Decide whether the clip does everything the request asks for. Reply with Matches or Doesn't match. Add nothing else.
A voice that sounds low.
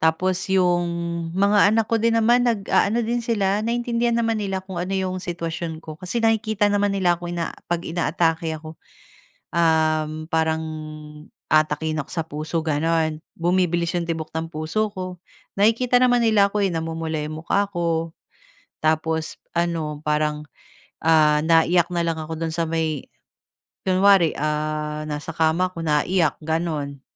Doesn't match